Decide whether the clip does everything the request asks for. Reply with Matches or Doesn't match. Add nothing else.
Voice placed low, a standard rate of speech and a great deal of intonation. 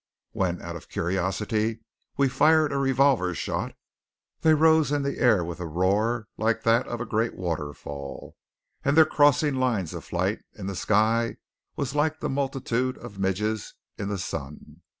Matches